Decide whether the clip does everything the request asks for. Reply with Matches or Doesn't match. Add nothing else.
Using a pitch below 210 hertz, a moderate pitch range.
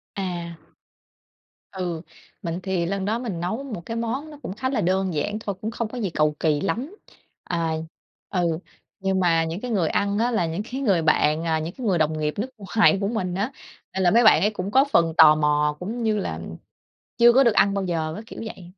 Matches